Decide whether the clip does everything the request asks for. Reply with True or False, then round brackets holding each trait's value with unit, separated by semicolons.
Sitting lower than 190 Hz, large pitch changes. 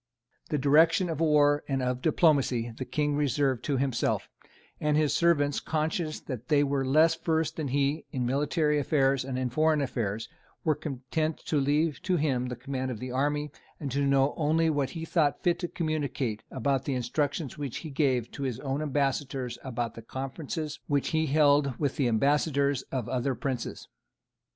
False (140 Hz; 2.8 semitones)